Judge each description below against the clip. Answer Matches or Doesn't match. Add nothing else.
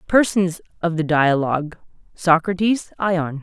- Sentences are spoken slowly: Matches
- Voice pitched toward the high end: Doesn't match